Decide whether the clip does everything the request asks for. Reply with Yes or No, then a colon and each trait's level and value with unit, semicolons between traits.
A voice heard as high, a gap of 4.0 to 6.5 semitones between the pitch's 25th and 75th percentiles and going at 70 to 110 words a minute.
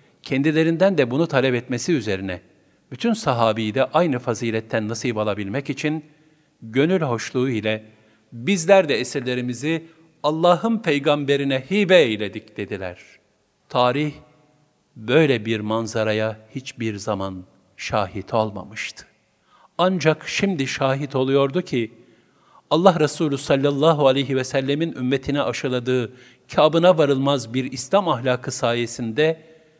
No: low, 135 Hz; average, 5.3 semitones; average, 105 wpm